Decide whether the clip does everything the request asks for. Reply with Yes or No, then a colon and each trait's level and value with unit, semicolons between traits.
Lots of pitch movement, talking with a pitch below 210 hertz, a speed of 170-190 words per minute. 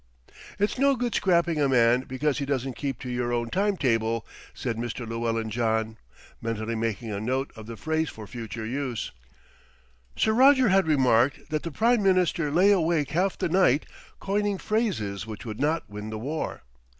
Yes: wide, 7.3 semitones; low, 135 Hz; average, 175 wpm